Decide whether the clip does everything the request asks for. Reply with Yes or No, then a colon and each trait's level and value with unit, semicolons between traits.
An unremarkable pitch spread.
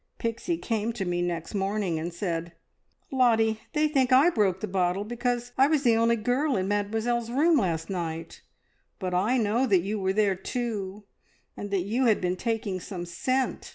Yes: average, 4.5 semitones